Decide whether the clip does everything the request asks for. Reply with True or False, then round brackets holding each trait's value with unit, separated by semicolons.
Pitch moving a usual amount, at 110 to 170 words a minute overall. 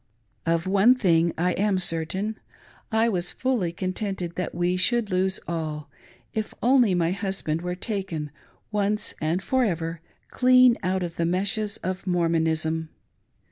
True (3.9 semitones; 145 wpm)